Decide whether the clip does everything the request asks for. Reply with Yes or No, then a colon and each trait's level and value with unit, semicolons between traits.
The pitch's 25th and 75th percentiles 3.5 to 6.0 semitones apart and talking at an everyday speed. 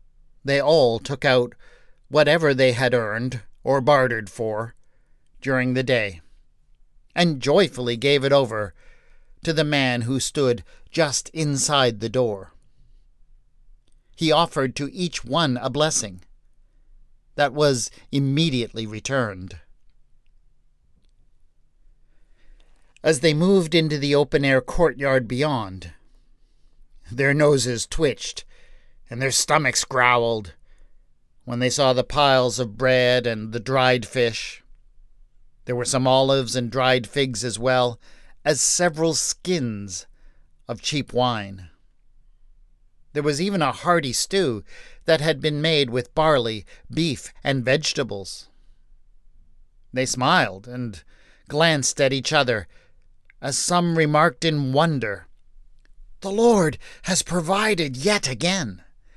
No: average, 4.7 semitones; slow, 115 wpm